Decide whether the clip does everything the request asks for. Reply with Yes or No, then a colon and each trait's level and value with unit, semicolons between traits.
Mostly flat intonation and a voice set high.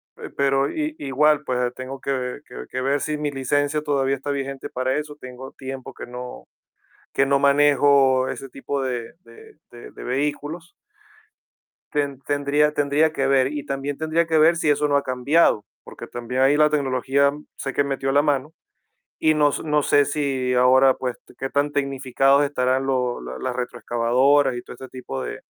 No: narrow, 2.1 semitones; low, 135 Hz